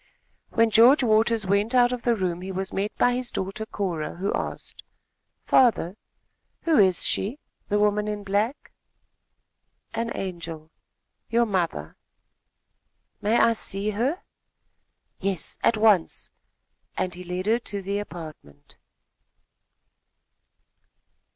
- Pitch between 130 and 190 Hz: No, high, 205 Hz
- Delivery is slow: Yes, slow, 120 wpm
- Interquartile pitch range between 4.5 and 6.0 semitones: No, average, 3.7 semitones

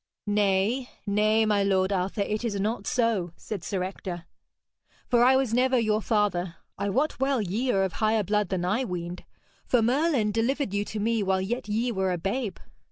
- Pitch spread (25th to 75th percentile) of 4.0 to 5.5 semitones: No, average, 3.5 semitones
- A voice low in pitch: No, high, 210 Hz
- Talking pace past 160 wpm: Yes, average, 190 wpm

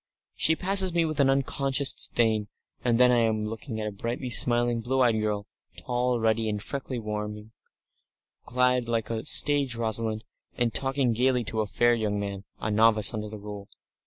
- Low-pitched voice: Yes, low, 115 Hz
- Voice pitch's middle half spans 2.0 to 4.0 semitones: Yes, average, 2.8 semitones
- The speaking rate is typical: Yes, average, 180 wpm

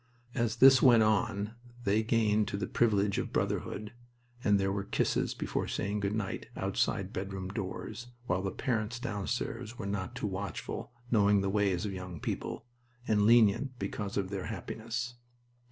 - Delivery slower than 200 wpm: Yes, average, 160 wpm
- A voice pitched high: No, low, 105 Hz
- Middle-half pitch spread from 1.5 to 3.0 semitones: Yes, narrow, 2.6 semitones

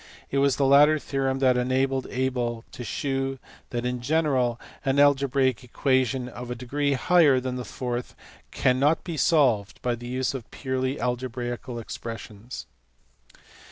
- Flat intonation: Yes, narrow, 1.9 semitones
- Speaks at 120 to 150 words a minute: Yes, average, 145 wpm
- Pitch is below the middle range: Yes, low, 130 Hz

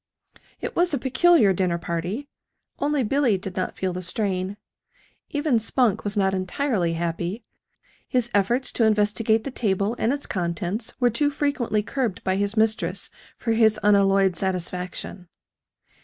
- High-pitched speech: Yes, high, 210 Hz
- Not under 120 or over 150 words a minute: Yes, average, 145 wpm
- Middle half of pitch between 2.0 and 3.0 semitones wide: No, average, 4.7 semitones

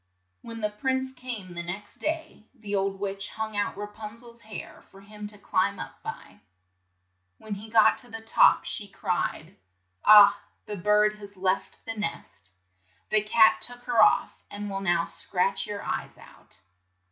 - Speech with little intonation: Yes, narrow, 2.1 semitones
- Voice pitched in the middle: No, high, 210 Hz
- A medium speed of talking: Yes, average, 170 wpm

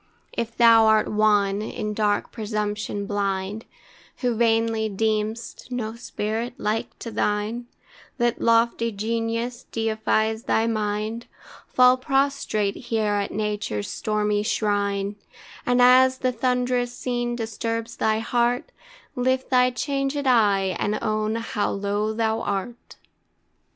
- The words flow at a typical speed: No, slow, 120 wpm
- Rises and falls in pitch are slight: Yes, narrow, 2.3 semitones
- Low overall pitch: No, high, 225 Hz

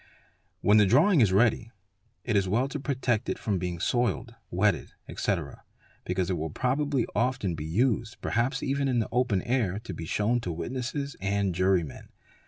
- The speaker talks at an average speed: Yes, average, 175 wpm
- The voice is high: No, low, 110 Hz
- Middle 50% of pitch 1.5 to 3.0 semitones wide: No, average, 5.2 semitones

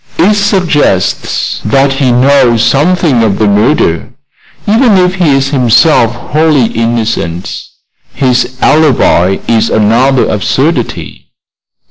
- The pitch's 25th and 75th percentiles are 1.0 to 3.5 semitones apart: No, wide, 5.4 semitones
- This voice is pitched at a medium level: No, low, 130 Hz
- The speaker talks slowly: Yes, slow, 105 wpm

